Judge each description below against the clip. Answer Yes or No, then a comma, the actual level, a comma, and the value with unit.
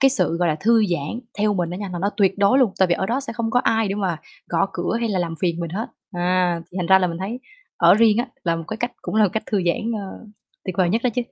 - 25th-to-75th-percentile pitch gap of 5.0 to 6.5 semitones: No, average, 4.2 semitones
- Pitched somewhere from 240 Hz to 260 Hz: No, high, 195 Hz